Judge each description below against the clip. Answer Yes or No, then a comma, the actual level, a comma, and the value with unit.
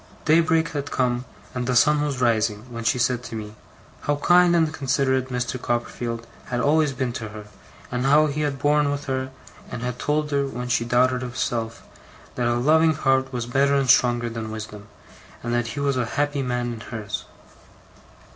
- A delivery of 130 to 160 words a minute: No, average, 185 wpm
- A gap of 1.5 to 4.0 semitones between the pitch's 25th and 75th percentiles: Yes, average, 3.1 semitones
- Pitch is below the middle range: Yes, low, 125 Hz